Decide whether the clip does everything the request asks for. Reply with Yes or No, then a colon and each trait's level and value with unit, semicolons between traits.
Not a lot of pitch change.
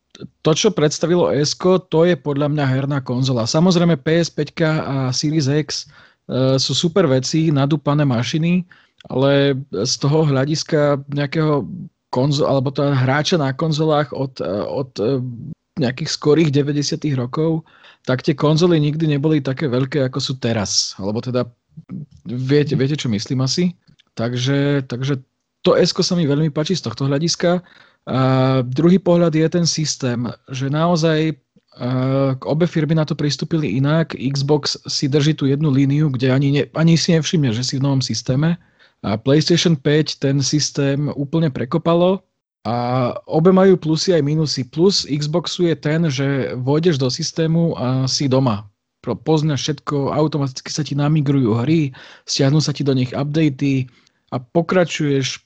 No: average, 3.3 semitones